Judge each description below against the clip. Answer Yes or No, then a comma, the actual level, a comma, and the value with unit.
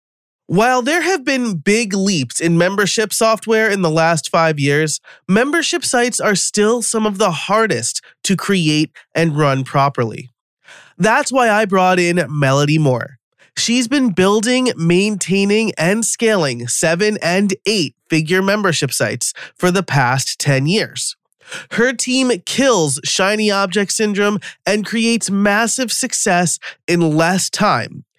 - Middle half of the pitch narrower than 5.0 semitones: No, wide, 5.4 semitones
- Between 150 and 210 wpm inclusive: No, slow, 135 wpm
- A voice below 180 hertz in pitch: No, high, 195 Hz